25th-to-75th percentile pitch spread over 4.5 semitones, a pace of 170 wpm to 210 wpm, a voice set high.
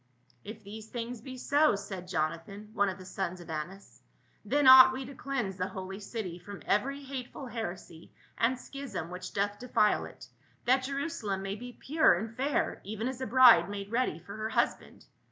Yes: average, 5.1 semitones; average, 190 wpm; high, 215 Hz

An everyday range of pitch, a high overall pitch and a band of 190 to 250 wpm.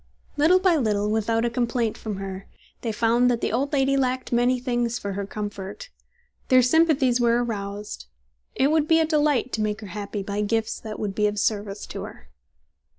Yes: average, 3.7 semitones; high, 230 Hz; average, 195 wpm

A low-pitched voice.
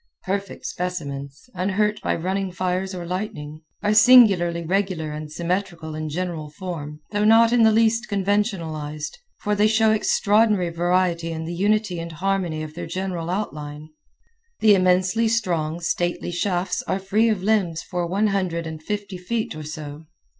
No: medium, 180 Hz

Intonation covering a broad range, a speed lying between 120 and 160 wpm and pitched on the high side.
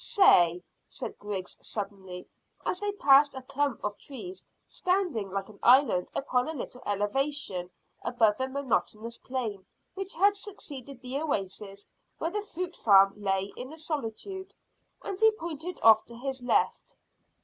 Yes: wide, 7.7 semitones; average, 150 wpm; very high, 260 Hz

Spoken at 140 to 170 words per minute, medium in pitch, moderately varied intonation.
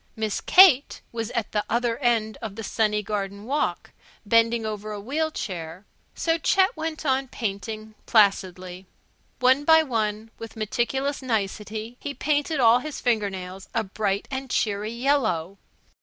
No: average, 150 wpm; high, 225 Hz; average, 4.3 semitones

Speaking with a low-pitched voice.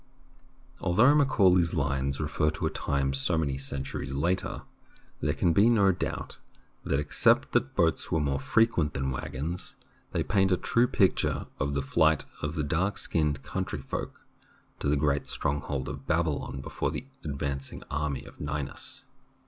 Yes: very low, 75 Hz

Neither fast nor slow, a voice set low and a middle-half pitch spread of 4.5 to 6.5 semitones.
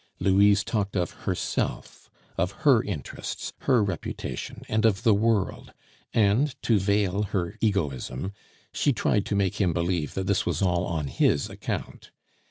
No: average, 150 wpm; low, 100 Hz; average, 3.0 semitones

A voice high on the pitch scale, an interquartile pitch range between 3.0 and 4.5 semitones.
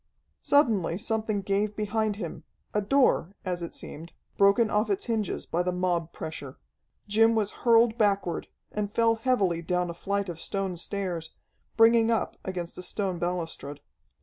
Yes: high, 200 Hz; average, 3.9 semitones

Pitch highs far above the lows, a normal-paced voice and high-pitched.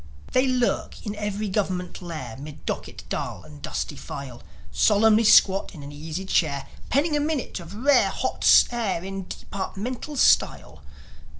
Yes: wide, 6.5 semitones; average, 145 wpm; high, 195 Hz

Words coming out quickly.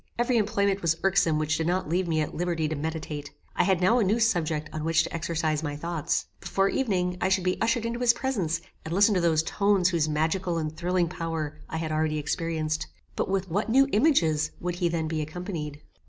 Yes: fast, 215 wpm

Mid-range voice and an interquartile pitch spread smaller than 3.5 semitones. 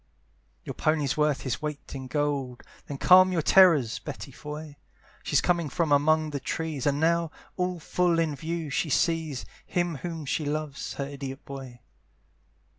Yes: medium, 150 Hz; average, 2.9 semitones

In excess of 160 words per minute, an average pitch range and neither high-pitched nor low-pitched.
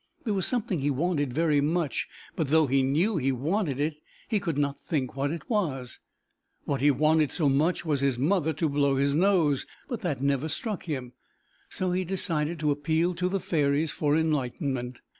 Yes: average, 190 wpm; average, 3.7 semitones; medium, 150 Hz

